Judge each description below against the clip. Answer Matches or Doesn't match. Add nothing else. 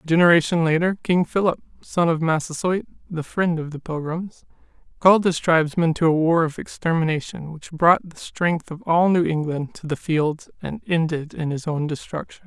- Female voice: Doesn't match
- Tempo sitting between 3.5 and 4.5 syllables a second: Doesn't match